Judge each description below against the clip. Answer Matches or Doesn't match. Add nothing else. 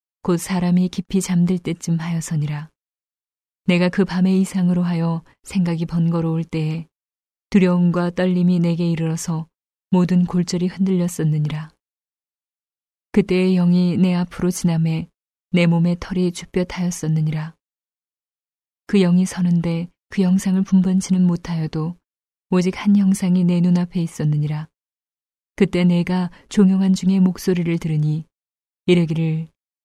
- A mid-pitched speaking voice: Matches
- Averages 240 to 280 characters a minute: Matches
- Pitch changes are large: Doesn't match